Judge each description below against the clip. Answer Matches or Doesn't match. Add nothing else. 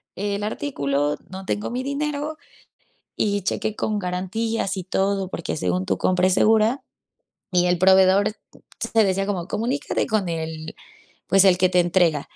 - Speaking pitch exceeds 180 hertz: Matches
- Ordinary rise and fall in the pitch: Matches